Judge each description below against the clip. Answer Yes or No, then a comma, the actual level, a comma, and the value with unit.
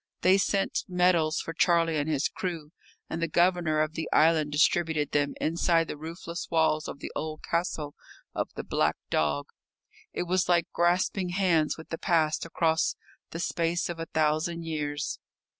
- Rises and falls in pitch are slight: Yes, narrow, 1.9 semitones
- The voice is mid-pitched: Yes, medium, 165 Hz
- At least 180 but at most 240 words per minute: No, average, 165 wpm